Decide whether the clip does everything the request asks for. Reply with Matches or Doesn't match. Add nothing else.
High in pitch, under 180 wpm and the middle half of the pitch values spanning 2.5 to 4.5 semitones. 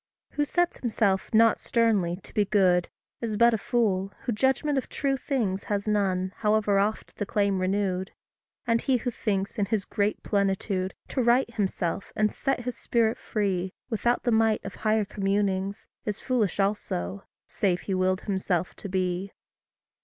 Matches